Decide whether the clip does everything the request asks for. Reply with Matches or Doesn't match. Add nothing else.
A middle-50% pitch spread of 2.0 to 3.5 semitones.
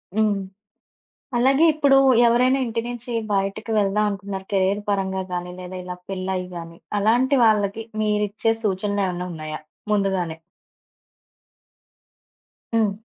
Matches